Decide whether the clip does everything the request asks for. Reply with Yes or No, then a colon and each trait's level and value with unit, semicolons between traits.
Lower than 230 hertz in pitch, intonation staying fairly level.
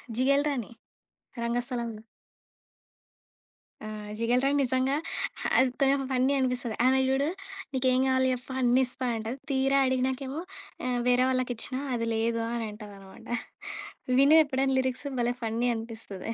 No: very high, 255 Hz; narrow, 2.1 semitones